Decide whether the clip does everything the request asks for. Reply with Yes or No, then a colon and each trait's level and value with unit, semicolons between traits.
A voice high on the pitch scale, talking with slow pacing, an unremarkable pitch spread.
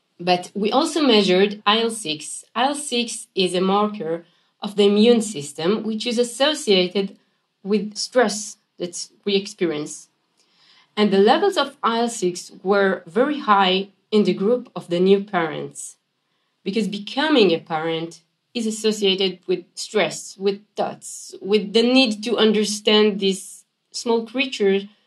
Yes: high, 205 Hz; slow, 130 wpm; average, 3.7 semitones